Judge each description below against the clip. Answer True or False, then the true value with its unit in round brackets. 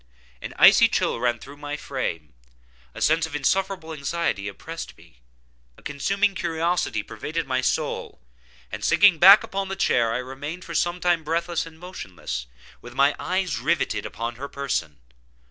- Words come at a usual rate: True (160 wpm)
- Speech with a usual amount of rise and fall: False (5.7 semitones)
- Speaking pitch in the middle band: True (150 Hz)